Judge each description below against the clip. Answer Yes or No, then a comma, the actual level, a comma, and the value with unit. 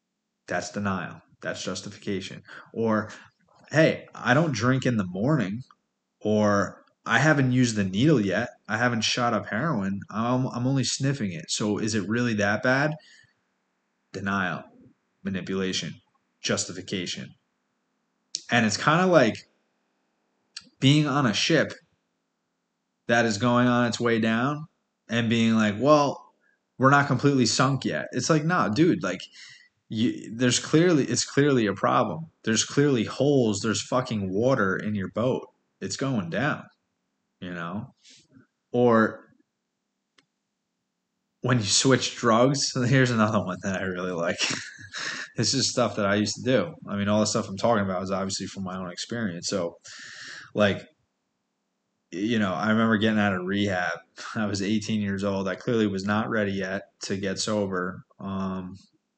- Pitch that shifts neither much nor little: Yes, average, 4.4 semitones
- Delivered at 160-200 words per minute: No, average, 150 wpm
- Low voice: Yes, low, 115 Hz